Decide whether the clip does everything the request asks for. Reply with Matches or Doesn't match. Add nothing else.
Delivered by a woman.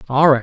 Doesn't match